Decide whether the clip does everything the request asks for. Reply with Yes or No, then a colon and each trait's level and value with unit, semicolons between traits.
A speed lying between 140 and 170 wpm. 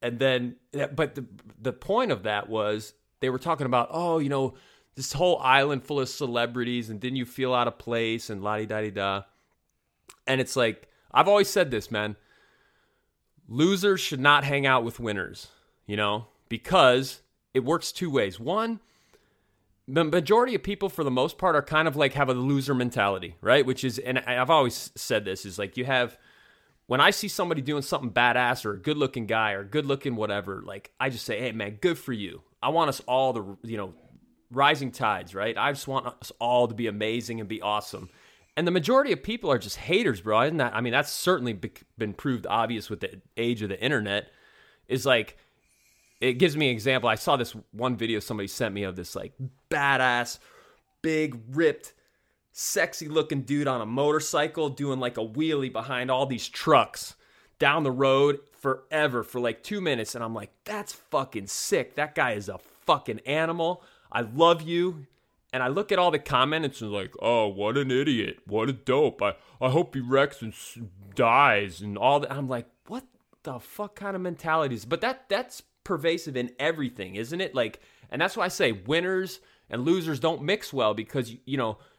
No: average, 195 wpm